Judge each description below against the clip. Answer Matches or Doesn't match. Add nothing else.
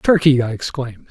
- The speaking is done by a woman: Doesn't match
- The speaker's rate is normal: Matches